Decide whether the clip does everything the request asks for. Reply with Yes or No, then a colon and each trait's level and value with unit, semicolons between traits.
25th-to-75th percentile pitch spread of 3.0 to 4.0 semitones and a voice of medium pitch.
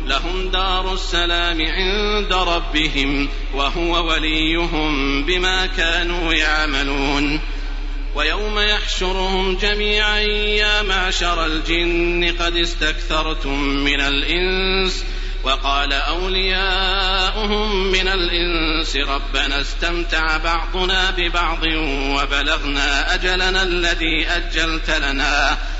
Yes: average, 3.6 semitones; medium, 170 Hz